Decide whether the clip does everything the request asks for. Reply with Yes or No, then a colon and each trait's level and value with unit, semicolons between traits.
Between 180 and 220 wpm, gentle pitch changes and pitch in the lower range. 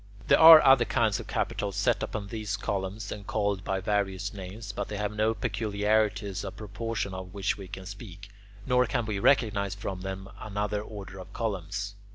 Yes: average, 190 wpm; narrow, 1.8 semitones; low, 100 Hz